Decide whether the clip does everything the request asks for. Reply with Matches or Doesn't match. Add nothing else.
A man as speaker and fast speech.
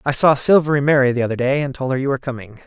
Matches